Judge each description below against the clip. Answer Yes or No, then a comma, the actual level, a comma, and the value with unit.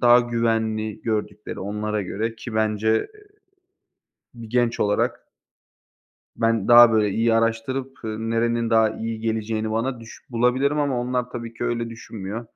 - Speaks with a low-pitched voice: Yes, low, 115 Hz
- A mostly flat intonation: Yes, narrow, 1.6 semitones